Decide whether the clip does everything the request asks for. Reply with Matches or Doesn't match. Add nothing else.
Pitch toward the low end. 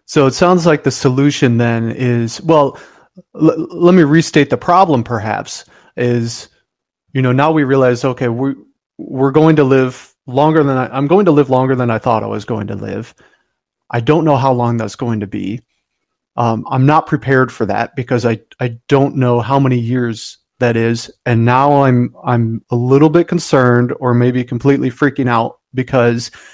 Matches